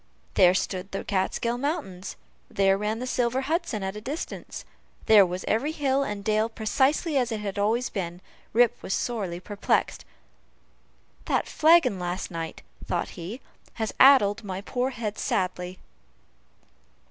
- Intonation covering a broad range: No, average, 4.8 semitones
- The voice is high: Yes, high, 215 Hz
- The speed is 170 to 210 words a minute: No, average, 145 wpm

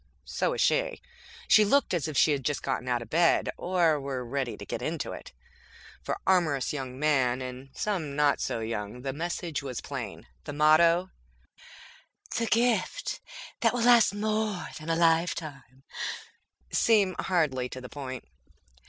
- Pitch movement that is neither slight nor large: No, wide, 6.0 semitones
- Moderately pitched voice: Yes, medium, 155 Hz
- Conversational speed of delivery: Yes, average, 160 wpm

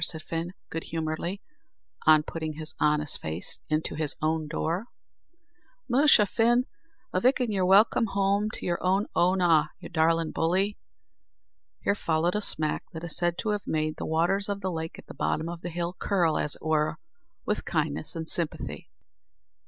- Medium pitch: Yes, medium, 170 Hz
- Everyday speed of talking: Yes, average, 170 wpm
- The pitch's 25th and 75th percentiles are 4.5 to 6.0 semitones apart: No, average, 3.8 semitones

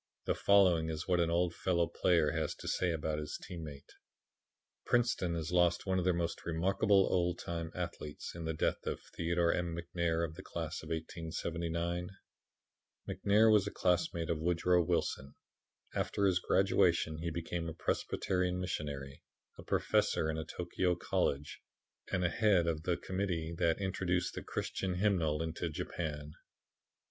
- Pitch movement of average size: No, narrow, 1.9 semitones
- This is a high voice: No, very low, 85 Hz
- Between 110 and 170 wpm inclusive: Yes, average, 160 wpm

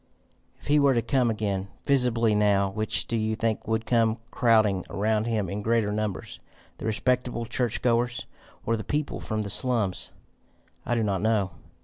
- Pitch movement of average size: No, narrow, 2.2 semitones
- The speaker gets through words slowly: No, average, 170 wpm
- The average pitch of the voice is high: No, low, 110 Hz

